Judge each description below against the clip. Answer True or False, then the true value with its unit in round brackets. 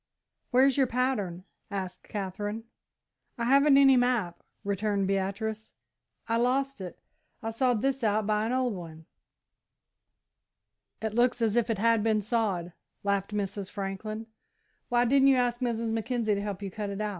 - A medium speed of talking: True (155 wpm)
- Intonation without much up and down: False (3.5 semitones)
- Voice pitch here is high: True (220 Hz)